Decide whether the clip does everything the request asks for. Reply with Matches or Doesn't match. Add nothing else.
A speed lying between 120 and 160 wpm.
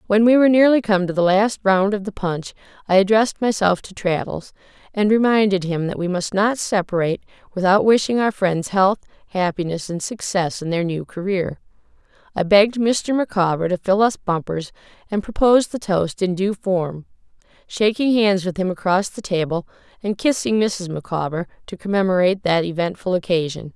Doesn't match